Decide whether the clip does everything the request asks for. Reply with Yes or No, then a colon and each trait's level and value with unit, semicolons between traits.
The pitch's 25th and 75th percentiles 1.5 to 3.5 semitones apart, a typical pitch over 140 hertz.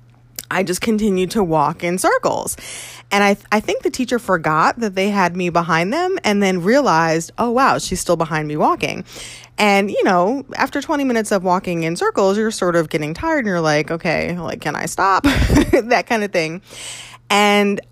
No: average, 4.9 semitones; high, 190 Hz